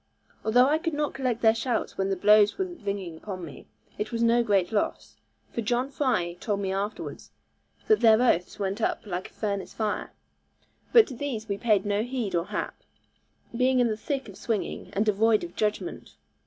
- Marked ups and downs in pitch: No, average, 3.6 semitones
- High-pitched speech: Yes, high, 215 Hz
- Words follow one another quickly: No, average, 195 wpm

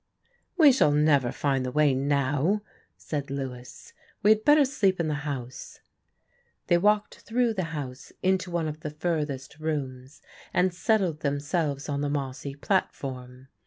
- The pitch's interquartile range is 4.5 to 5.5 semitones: Yes, average, 4.9 semitones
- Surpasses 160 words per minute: No, average, 150 wpm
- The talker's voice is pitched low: No, medium, 150 Hz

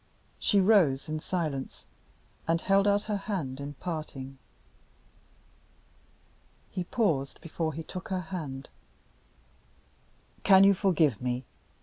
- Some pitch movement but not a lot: No, wide, 5.8 semitones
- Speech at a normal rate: No, slow, 110 wpm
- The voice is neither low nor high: Yes, medium, 165 Hz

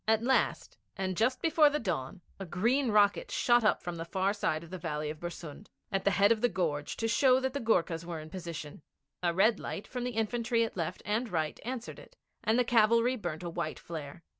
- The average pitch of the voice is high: Yes, high, 200 Hz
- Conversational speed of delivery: No, fast, 225 wpm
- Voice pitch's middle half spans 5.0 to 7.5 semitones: Yes, wide, 5.6 semitones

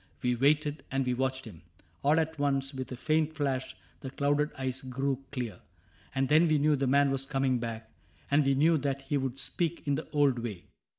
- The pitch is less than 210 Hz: Yes, low, 135 Hz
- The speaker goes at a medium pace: No, fast, 210 wpm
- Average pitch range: No, narrow, 2.1 semitones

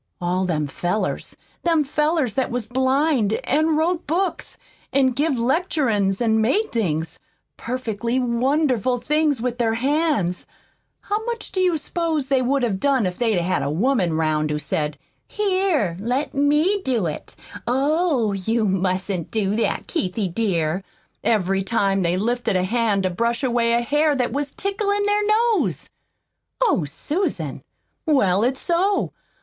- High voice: Yes, high, 245 Hz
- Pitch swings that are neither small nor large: No, wide, 7.7 semitones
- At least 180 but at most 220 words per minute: No, average, 150 wpm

